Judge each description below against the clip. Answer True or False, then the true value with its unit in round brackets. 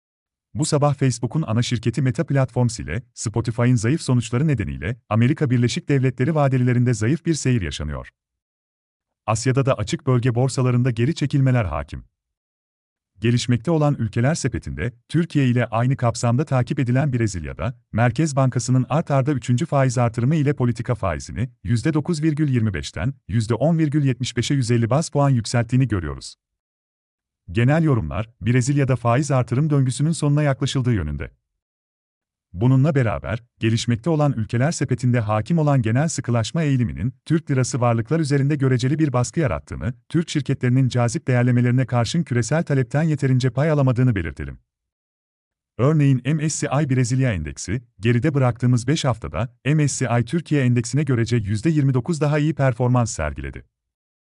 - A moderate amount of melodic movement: True (3.9 semitones)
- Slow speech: False (125 wpm)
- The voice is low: True (125 Hz)